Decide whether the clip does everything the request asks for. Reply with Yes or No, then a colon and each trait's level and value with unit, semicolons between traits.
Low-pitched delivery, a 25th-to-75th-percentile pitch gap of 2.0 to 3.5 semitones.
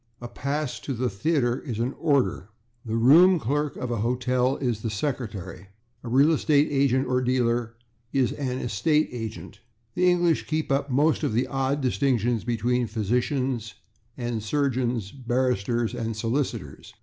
Yes: low, 125 Hz; average, 3.1 semitones